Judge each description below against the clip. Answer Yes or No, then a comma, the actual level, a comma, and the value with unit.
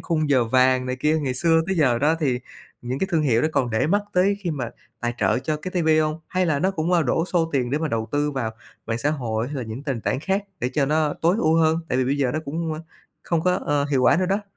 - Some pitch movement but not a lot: Yes, average, 4.3 semitones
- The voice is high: No, medium, 150 Hz